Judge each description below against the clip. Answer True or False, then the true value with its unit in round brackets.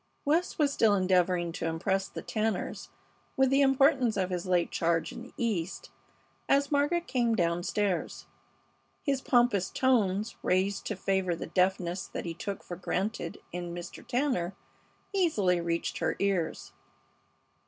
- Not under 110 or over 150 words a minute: True (145 wpm)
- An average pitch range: False (6.0 semitones)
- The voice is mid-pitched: False (195 Hz)